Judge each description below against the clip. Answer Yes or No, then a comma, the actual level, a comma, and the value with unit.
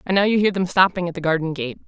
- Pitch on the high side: No, medium, 175 Hz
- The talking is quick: Yes, fast, 320 wpm